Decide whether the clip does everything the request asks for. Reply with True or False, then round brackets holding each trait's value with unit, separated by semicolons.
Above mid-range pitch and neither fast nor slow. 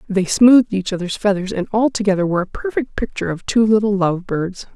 True (200 Hz; 190 wpm)